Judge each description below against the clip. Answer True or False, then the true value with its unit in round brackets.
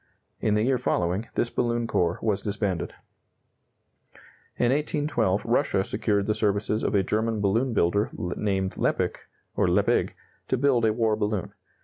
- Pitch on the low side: True (105 Hz)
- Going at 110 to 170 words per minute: True (145 wpm)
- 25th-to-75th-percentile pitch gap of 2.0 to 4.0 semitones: True (2.9 semitones)